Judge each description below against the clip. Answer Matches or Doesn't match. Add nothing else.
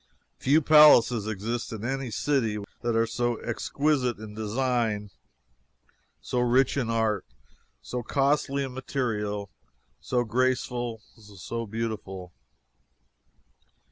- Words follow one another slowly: Matches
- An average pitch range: Matches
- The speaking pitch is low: Matches